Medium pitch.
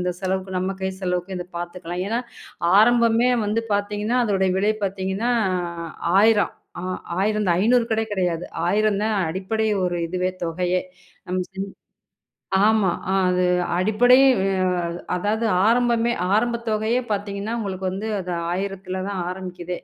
No: high, 195 Hz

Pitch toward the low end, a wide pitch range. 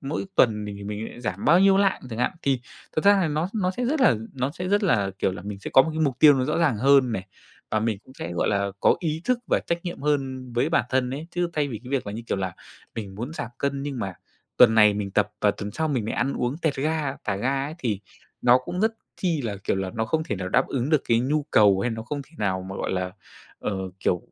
Yes: low, 130 Hz; wide, 6.6 semitones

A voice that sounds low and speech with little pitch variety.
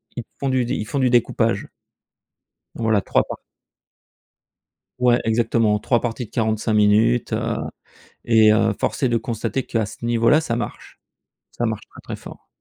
Yes: low, 115 Hz; narrow, 1.8 semitones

